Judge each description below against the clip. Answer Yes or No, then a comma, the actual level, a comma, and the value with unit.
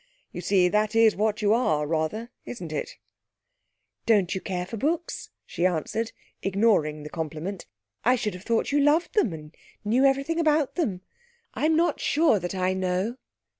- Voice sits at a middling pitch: No, high, 210 Hz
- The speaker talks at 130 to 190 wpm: Yes, average, 170 wpm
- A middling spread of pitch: No, wide, 6.0 semitones